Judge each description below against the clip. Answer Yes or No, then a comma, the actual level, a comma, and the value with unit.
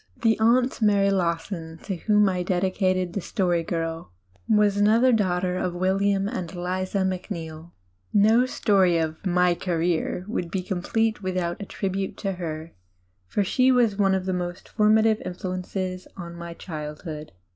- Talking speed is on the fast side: No, average, 150 wpm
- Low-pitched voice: No, medium, 185 Hz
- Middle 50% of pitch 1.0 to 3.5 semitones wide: Yes, average, 2.8 semitones